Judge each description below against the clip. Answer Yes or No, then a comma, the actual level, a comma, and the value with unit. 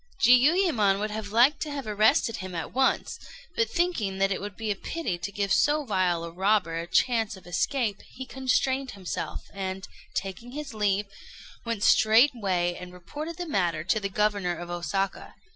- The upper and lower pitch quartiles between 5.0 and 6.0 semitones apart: Yes, wide, 5.4 semitones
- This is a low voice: No, high, 210 Hz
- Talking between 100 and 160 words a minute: No, average, 175 wpm